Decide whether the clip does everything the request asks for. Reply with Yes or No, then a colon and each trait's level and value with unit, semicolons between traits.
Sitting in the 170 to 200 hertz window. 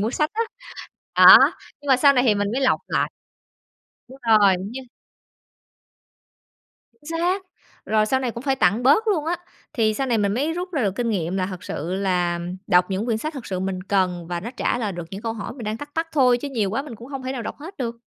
No: high, 230 Hz